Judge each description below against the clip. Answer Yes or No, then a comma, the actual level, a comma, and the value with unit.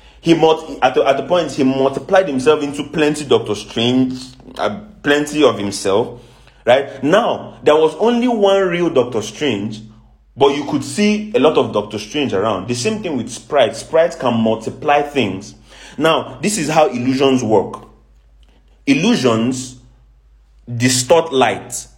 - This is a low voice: Yes, low, 130 Hz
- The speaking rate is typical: Yes, average, 150 wpm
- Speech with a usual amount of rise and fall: No, wide, 6.6 semitones